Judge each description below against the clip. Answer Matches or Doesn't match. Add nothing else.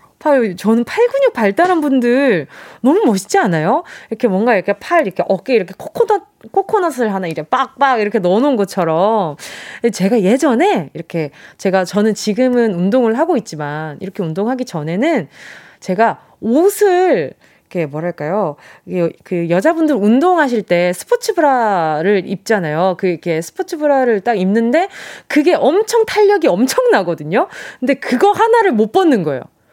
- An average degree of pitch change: Doesn't match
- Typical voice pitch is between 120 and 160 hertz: Doesn't match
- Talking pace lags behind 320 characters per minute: Doesn't match